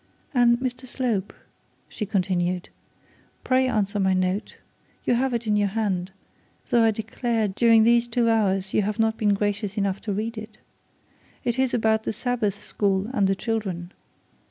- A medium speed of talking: Yes, average, 165 wpm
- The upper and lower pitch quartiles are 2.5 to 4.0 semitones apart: Yes, average, 3.1 semitones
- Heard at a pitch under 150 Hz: No, high, 215 Hz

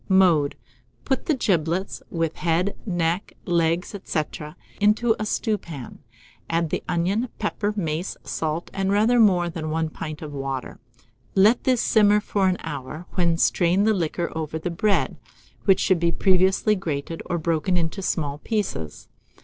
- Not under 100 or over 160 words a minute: Yes, average, 155 wpm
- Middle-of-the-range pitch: Yes, medium, 175 Hz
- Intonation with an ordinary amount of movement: Yes, average, 3.8 semitones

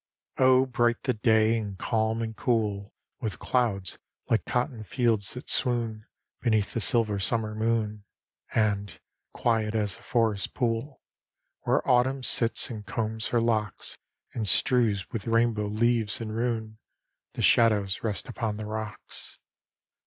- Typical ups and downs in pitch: No, narrow, 1.9 semitones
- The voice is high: No, low, 110 Hz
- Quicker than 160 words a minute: No, average, 140 wpm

